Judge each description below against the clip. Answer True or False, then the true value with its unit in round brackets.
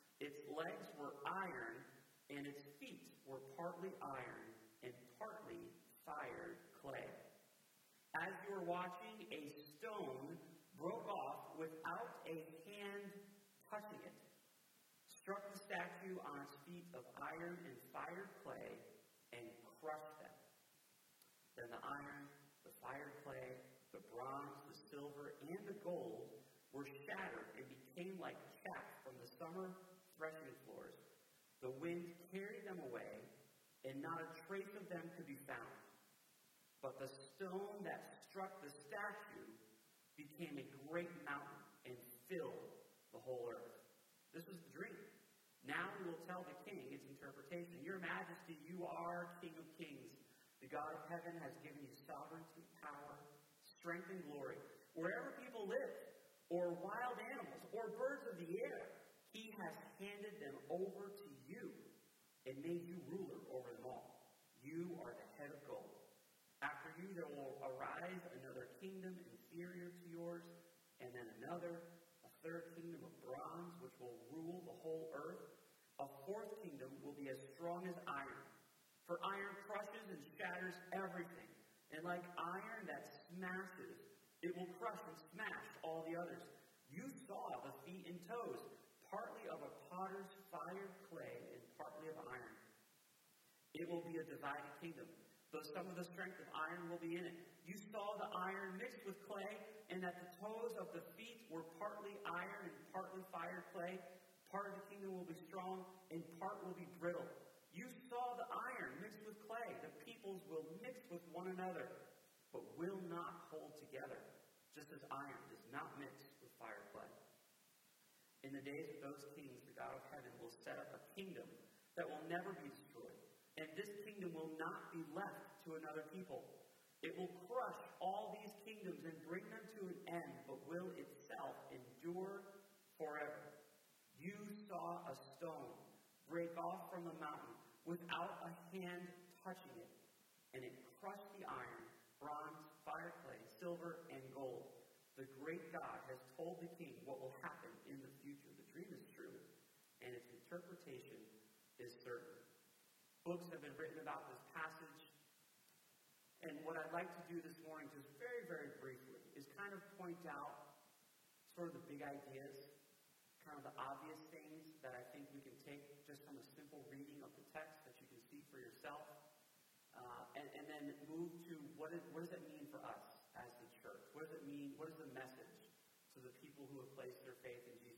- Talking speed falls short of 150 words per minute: False (160 wpm)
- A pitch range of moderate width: True (4.4 semitones)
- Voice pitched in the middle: True (170 Hz)